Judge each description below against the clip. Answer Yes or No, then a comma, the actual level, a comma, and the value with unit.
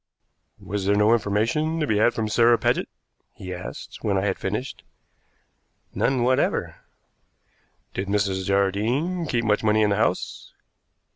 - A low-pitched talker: Yes, low, 105 Hz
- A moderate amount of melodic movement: Yes, average, 3.3 semitones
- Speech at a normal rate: Yes, average, 145 wpm